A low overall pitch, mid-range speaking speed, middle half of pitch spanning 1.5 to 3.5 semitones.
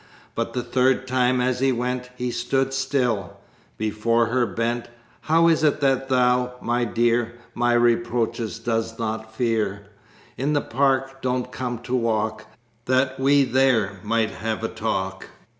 Yes: low, 120 Hz; average, 150 wpm; narrow, 2.4 semitones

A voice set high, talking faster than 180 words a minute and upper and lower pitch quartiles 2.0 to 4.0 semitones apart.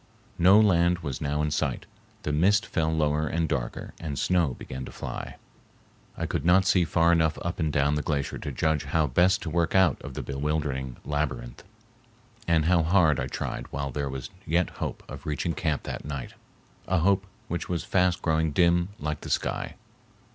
No: very low, 80 Hz; average, 190 wpm; average, 3.1 semitones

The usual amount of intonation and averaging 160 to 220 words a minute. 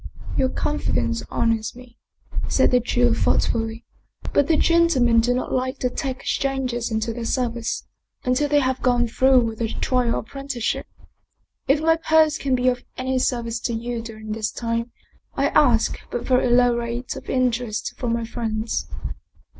No: narrow, 2.1 semitones; average, 170 wpm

